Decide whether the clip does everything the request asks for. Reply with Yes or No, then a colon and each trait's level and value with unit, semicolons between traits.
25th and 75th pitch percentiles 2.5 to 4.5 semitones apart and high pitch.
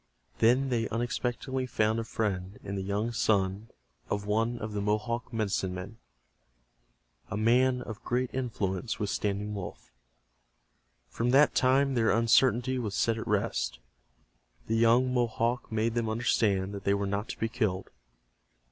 No: average, 2.9 semitones; low, 110 Hz